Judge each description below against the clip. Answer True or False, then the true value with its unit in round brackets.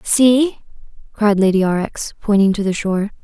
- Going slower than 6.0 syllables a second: True (5.0 syllables/s)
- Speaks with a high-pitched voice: True (210 Hz)